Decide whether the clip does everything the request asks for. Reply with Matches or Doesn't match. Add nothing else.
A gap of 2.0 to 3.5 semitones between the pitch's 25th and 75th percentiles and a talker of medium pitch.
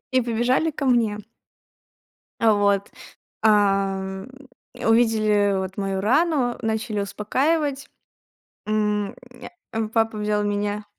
Doesn't match